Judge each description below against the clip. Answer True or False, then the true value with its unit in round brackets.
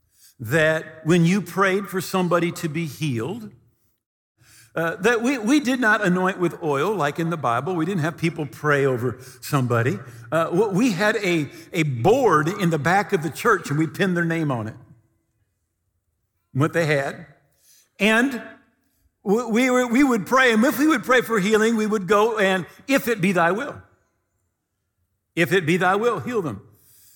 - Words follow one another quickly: False (175 wpm)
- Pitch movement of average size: False (7.0 semitones)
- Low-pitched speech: False (170 Hz)